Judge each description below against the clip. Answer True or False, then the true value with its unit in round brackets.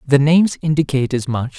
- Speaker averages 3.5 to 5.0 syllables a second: False (6.0 syllables/s)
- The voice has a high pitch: False (140 Hz)